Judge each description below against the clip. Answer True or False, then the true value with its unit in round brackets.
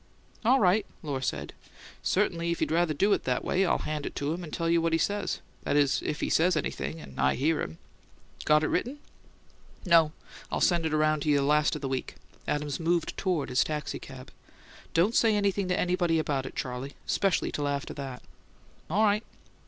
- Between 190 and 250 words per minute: True (200 wpm)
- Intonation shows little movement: False (4.1 semitones)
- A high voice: False (155 Hz)